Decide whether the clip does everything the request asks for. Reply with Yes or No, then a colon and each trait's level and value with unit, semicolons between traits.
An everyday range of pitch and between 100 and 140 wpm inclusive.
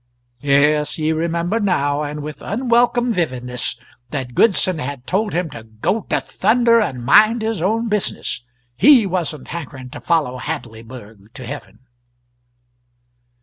No: wide, 8.5 semitones; slow, 135 wpm